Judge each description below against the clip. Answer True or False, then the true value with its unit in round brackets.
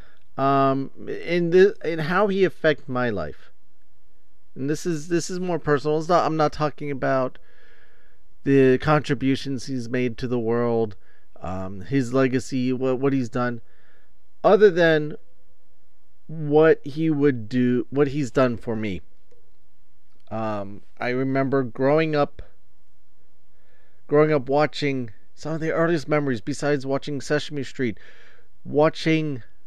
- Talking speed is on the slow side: True (130 wpm)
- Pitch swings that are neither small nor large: True (3.5 semitones)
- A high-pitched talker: False (135 Hz)